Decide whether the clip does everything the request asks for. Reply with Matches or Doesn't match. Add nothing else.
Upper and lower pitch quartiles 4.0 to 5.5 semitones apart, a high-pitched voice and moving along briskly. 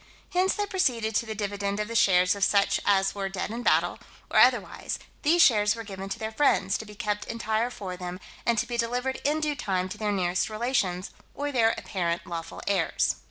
Doesn't match